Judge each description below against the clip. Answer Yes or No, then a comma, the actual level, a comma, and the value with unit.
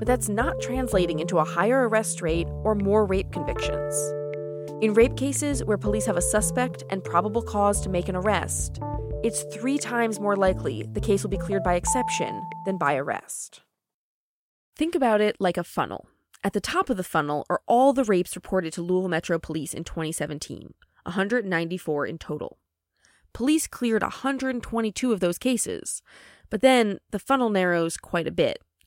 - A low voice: No, medium, 180 Hz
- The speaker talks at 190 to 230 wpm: No, average, 175 wpm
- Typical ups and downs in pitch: No, wide, 6.8 semitones